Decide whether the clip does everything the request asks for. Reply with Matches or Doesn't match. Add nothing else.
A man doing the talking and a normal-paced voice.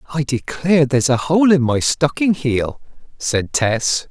Matches